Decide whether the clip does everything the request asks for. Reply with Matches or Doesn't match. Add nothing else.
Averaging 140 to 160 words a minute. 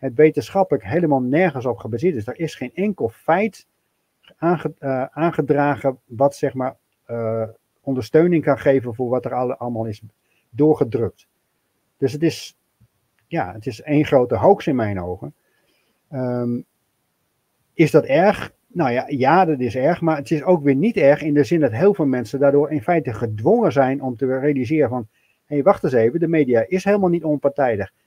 Doesn't match